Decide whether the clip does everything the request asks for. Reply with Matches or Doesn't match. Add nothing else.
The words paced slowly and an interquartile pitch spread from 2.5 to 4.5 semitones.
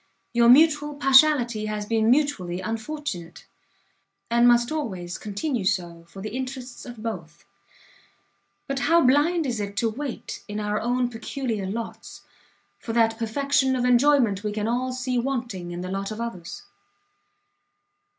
Doesn't match